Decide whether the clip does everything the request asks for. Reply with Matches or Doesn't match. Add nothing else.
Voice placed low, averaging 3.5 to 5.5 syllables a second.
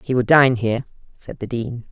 Matches